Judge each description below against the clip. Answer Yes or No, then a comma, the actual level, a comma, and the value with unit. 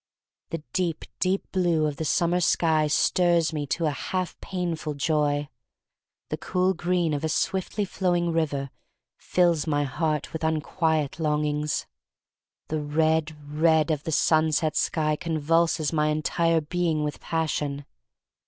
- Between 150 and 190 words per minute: No, slow, 135 wpm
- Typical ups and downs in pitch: No, narrow, 2.2 semitones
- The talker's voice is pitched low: No, medium, 160 Hz